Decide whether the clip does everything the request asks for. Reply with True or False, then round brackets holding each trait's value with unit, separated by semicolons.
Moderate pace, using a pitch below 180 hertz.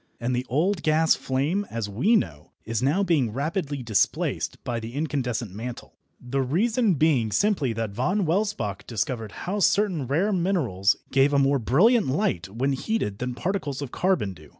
True (170 wpm; 135 Hz)